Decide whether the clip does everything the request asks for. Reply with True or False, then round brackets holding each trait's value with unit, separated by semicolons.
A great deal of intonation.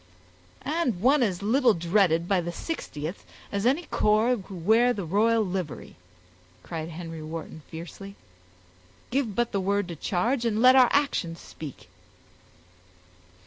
True (5.8 semitones)